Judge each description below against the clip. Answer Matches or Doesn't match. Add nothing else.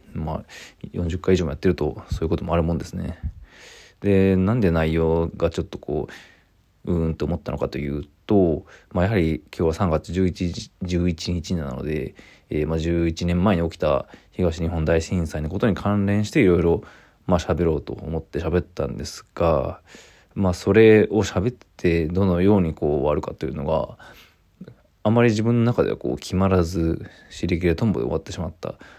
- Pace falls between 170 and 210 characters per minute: Doesn't match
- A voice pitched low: Matches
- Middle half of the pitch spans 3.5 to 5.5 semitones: Doesn't match